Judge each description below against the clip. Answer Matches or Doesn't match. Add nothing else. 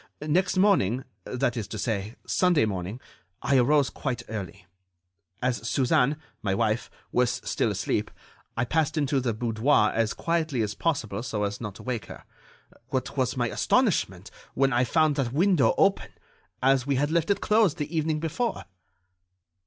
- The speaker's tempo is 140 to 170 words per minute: Matches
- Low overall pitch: Matches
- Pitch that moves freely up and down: Matches